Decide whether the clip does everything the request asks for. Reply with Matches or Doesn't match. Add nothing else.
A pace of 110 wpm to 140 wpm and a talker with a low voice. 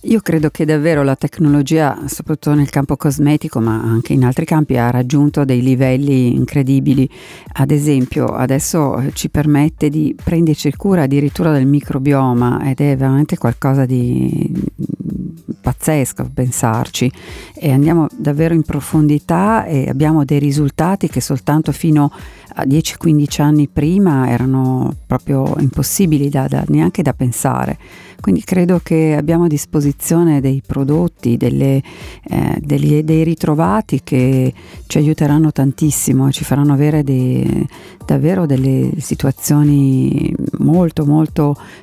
Doesn't match